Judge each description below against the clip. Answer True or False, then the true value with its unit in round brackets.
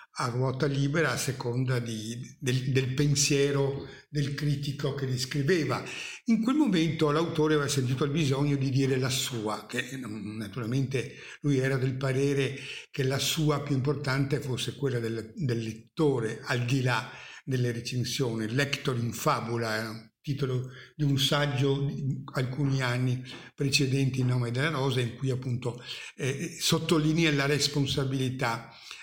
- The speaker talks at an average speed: True (145 wpm)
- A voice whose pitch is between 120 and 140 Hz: True (135 Hz)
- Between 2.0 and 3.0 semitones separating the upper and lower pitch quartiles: True (2.5 semitones)